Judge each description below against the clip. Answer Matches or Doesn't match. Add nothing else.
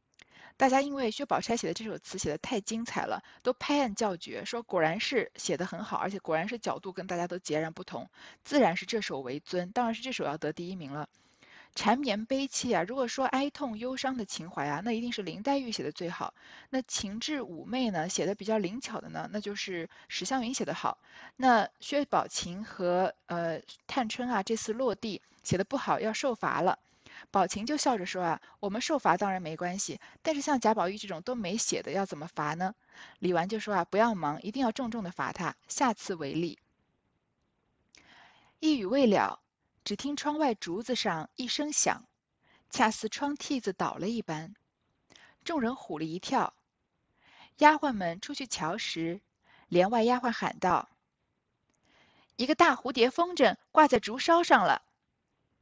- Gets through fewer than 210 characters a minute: Doesn't match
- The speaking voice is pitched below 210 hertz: Doesn't match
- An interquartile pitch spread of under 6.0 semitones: Doesn't match